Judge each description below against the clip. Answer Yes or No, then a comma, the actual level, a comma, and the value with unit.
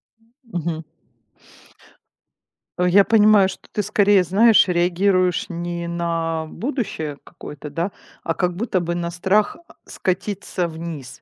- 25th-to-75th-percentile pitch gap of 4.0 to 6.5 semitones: No, average, 3.1 semitones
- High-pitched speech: No, medium, 180 Hz